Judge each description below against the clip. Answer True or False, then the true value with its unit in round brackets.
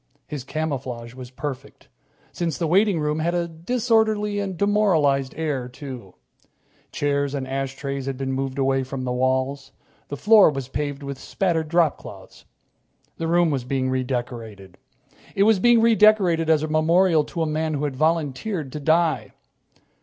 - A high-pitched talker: False (150 Hz)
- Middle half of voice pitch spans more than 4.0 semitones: True (4.4 semitones)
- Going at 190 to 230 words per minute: False (155 wpm)